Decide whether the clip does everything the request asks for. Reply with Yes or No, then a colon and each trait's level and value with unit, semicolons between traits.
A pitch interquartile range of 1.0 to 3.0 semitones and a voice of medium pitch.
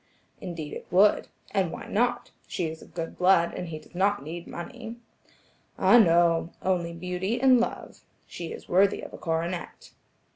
Yes: narrow, 2.6 semitones; medium, 175 Hz